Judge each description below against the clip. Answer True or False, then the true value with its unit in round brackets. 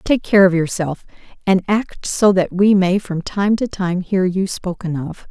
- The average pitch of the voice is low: False (190 Hz)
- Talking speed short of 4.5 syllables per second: True (4.2 syllables/s)